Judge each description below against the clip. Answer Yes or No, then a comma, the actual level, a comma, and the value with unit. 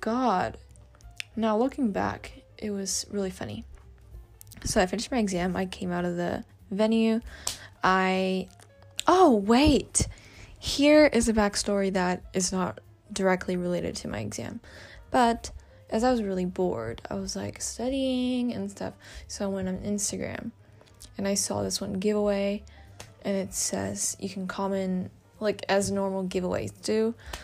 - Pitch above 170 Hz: Yes, high, 190 Hz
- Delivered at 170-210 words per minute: No, average, 150 wpm